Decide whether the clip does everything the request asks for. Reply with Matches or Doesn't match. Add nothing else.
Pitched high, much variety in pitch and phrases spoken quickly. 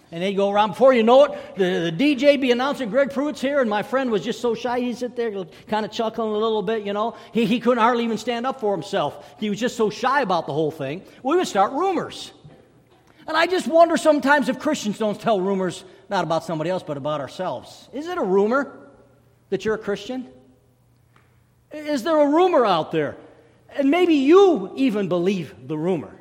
Matches